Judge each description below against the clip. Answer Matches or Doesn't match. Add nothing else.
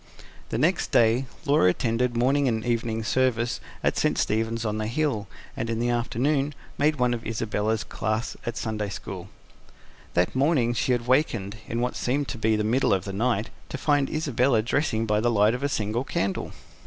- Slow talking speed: Doesn't match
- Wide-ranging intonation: Doesn't match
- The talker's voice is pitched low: Matches